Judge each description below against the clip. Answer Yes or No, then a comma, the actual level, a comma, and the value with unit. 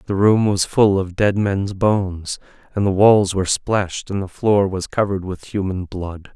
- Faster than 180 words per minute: Yes, average, 200 wpm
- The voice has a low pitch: Yes, very low, 95 Hz